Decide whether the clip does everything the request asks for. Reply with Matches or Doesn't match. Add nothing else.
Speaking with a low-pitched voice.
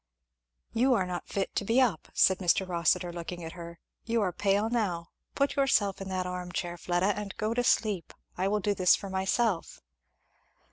Doesn't match